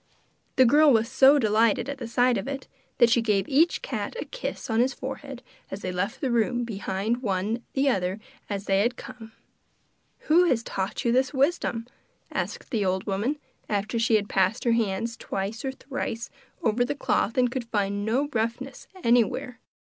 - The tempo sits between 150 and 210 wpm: Yes, average, 185 wpm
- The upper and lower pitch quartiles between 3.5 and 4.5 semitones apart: Yes, average, 3.9 semitones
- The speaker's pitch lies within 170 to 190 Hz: No, high, 235 Hz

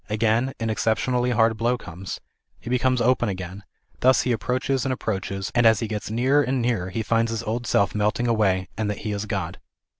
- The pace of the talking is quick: Yes, fast, 210 wpm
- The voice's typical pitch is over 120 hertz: No, low, 115 Hz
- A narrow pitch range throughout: No, average, 3.2 semitones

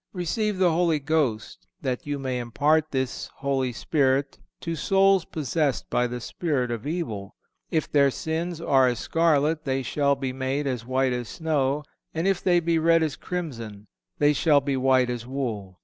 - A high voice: No, medium, 140 Hz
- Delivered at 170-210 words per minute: Yes, average, 175 wpm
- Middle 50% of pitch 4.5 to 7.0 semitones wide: No, average, 4.0 semitones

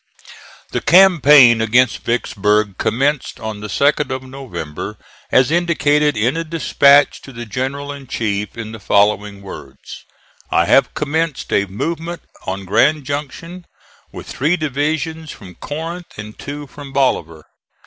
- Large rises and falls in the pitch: Yes, wide, 6.0 semitones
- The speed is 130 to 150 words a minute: Yes, average, 140 wpm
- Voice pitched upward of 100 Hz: Yes, low, 135 Hz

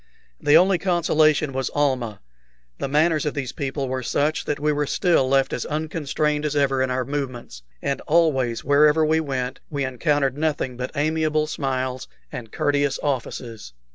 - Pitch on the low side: No, medium, 145 Hz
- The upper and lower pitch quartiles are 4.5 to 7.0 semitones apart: No, average, 2.8 semitones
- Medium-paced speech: Yes, average, 165 wpm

